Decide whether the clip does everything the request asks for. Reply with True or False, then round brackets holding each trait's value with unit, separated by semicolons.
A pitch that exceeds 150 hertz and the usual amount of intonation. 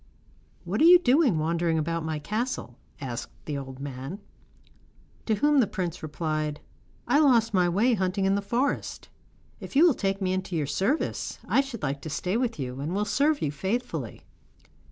False (190 Hz; 7.7 semitones)